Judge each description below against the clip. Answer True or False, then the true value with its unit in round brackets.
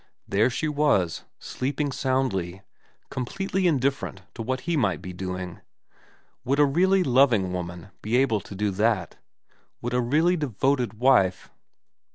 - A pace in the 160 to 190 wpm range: False (145 wpm)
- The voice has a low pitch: True (125 Hz)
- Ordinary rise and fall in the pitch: False (6.4 semitones)